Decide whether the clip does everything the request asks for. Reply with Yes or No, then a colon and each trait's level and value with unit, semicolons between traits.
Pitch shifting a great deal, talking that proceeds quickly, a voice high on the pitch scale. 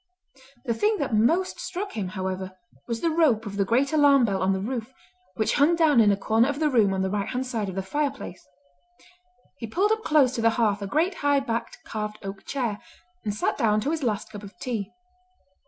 Yes: wide, 5.9 semitones; fast, 220 wpm; high, 230 Hz